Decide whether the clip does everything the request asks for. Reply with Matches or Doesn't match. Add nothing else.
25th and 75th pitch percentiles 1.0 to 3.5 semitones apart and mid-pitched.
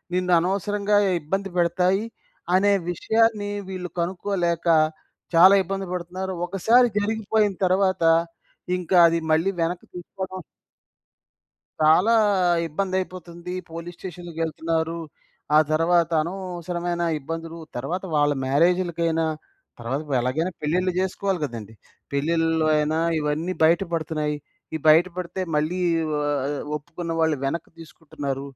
Matches